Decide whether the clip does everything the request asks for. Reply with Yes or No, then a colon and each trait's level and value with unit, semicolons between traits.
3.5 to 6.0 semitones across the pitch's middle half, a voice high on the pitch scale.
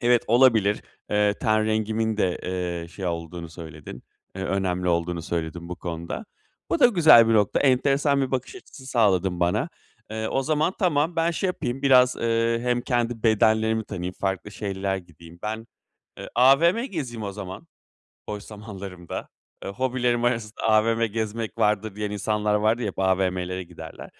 No: average, 4.4 semitones; low, 110 Hz